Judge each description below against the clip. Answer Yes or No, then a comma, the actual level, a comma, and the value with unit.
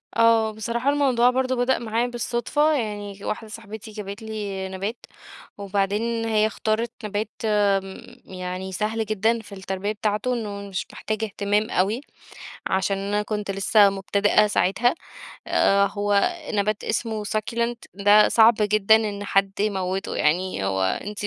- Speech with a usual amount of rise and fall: No, narrow, 2.2 semitones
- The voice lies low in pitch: No, high, 210 Hz